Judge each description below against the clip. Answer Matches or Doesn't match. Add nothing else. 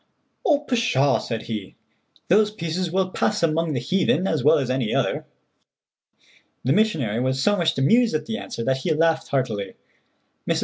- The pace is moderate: Matches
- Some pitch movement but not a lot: Doesn't match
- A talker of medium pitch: Matches